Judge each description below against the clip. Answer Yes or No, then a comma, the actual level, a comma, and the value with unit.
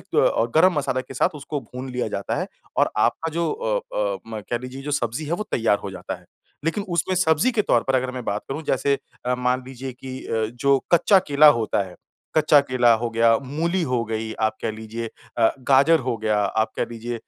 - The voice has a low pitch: Yes, low, 130 Hz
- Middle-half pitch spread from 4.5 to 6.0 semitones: Yes, average, 5.0 semitones